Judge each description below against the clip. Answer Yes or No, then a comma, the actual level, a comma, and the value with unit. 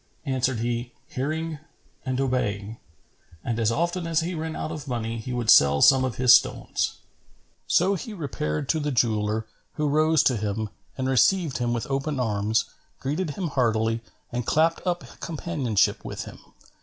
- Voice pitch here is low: Yes, low, 130 Hz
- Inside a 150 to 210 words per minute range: Yes, average, 165 wpm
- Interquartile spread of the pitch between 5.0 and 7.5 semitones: Yes, wide, 5.5 semitones